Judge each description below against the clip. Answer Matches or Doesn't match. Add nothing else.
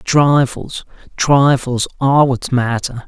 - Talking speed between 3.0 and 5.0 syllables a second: Matches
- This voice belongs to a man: Matches